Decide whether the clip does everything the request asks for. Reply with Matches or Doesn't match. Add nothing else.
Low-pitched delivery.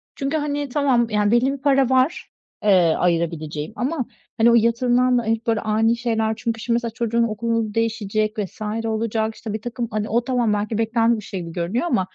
Doesn't match